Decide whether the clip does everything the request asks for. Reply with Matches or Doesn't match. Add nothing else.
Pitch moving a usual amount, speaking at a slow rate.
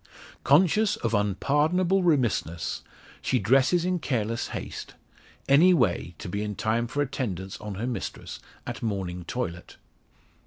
Doesn't match